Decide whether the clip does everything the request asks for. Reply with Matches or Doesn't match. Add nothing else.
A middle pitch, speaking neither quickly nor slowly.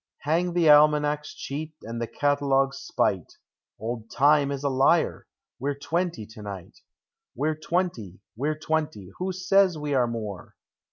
Matches